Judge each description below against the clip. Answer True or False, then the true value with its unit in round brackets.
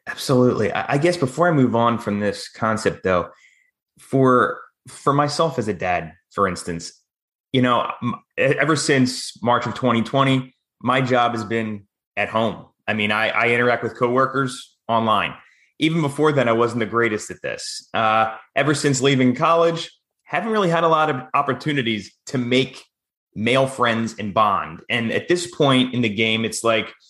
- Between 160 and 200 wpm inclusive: True (170 wpm)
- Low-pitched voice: True (125 Hz)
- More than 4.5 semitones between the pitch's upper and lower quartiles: False (3.9 semitones)